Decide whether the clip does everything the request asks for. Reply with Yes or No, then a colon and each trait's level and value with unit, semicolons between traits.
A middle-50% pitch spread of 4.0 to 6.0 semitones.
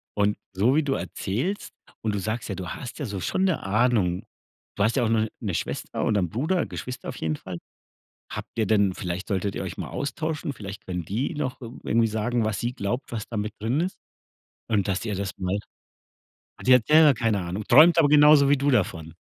Yes: wide, 5.5 semitones